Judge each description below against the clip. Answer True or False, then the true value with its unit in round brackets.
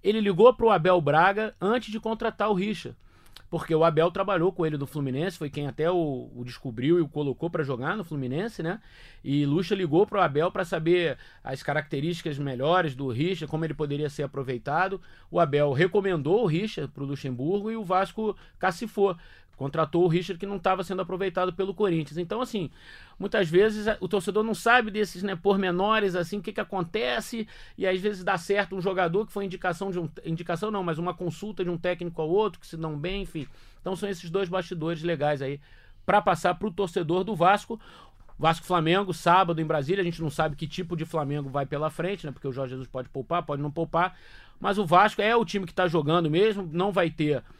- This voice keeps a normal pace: False (210 wpm)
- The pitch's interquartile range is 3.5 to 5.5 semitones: True (4.1 semitones)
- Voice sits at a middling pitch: True (180 Hz)